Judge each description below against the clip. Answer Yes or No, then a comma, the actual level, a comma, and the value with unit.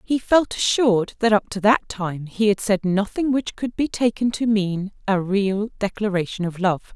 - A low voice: No, high, 210 Hz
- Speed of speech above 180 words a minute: Yes, average, 200 wpm